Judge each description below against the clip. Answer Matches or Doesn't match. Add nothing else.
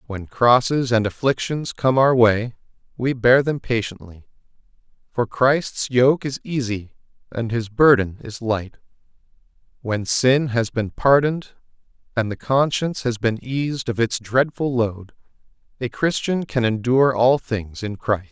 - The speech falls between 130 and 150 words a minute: Matches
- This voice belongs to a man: Matches